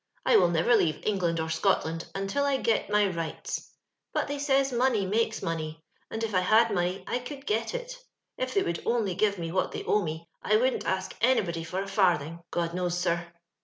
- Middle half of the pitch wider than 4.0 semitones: Yes, wide, 5.5 semitones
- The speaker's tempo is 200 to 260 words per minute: Yes, fast, 205 wpm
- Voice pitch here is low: No, high, 195 Hz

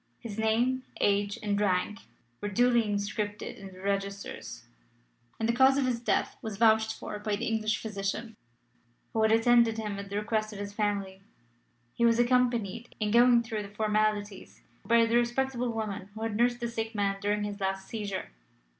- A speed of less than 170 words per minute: No, average, 180 wpm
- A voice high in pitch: Yes, high, 215 Hz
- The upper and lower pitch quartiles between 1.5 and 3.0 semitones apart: Yes, narrow, 2.4 semitones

